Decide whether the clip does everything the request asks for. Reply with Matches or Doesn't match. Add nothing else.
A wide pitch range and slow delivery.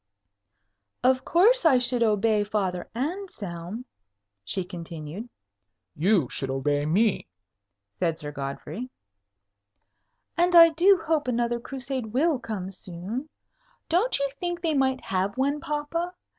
Matches